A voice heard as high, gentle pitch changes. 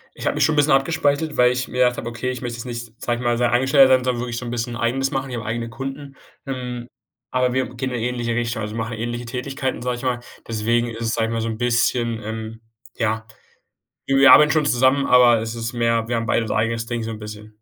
No: low, 120 Hz; narrow, 1.9 semitones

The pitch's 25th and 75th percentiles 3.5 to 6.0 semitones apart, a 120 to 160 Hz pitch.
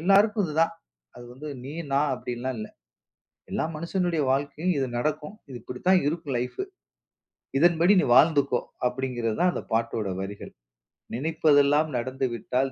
Yes: average, 4.7 semitones; medium, 140 Hz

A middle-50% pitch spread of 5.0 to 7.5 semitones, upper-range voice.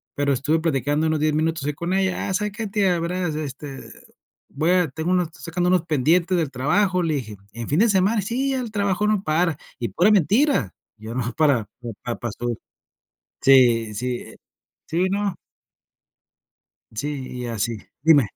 No: wide, 5.6 semitones; medium, 160 Hz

